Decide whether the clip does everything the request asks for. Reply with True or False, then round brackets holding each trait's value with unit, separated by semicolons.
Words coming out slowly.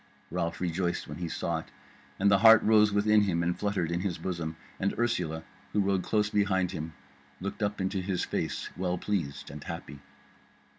False (185 wpm)